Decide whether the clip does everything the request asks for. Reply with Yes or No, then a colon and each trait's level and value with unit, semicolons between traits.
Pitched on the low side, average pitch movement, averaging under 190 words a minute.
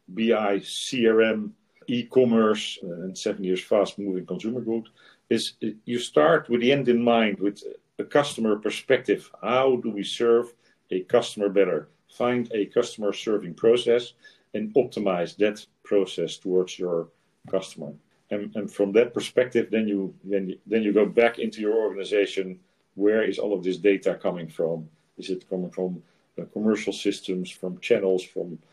Yes: low, 110 Hz; average, 4.0 semitones; average, 150 wpm